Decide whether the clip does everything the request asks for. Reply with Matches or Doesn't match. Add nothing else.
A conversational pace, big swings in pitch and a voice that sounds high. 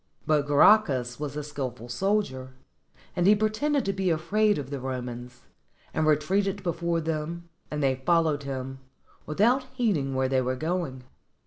Doesn't match